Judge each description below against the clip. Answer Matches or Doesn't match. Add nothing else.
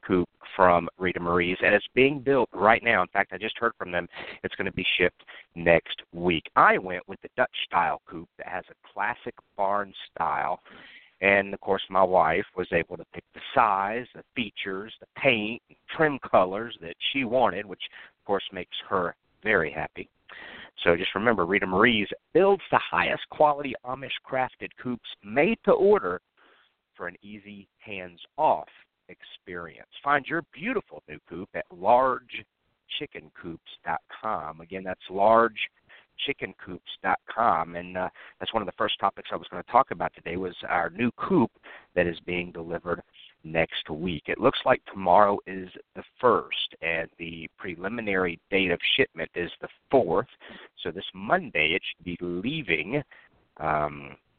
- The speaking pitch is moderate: Doesn't match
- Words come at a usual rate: Matches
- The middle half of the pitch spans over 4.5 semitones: Matches